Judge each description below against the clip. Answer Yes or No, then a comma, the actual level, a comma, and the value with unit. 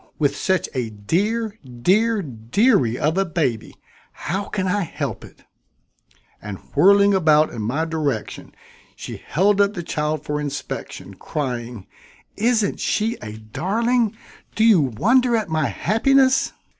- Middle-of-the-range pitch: Yes, medium, 170 Hz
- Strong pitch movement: Yes, wide, 7.6 semitones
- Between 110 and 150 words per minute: Yes, slow, 135 wpm